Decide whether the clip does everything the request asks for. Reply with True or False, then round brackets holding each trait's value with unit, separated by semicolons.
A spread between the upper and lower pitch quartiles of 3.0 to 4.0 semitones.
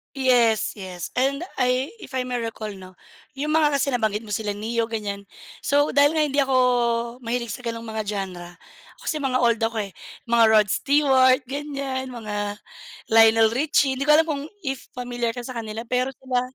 True (3.6 semitones)